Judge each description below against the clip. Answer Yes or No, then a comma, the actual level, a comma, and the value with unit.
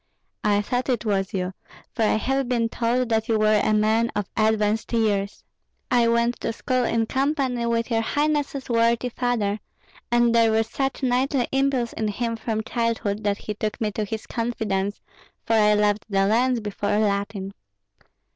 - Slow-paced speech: No, average, 175 wpm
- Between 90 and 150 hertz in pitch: No, high, 225 Hz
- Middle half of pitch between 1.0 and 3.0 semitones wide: Yes, narrow, 2.5 semitones